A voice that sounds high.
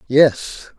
No: low, 135 Hz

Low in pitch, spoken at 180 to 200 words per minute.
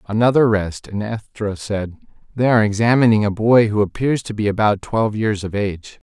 Yes: low, 105 Hz; average, 185 wpm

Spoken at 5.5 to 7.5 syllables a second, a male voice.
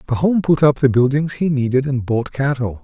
No: 5.2 syllables/s; male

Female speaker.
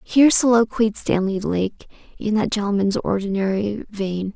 Yes: female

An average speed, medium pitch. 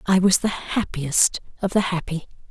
Yes: average, 165 wpm; medium, 180 Hz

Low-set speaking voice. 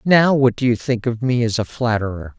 Yes: low, 120 Hz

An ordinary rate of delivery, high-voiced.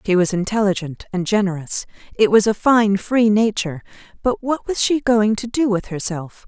Yes: average, 185 wpm; high, 210 Hz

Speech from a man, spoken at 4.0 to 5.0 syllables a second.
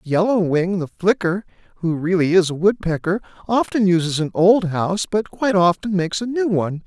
No: male; 5.4 syllables/s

